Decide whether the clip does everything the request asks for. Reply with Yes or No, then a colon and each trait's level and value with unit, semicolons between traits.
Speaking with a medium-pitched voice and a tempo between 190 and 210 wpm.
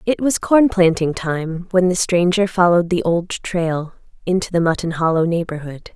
No: medium, 175 Hz; average, 170 wpm